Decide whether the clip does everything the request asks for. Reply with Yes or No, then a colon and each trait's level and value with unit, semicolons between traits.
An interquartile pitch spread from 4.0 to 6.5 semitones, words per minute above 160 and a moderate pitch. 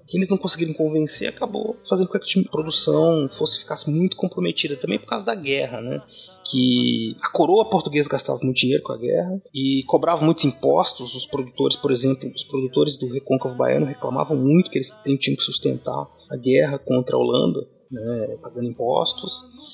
Yes: wide, 5.6 semitones; average, 180 wpm; medium, 145 Hz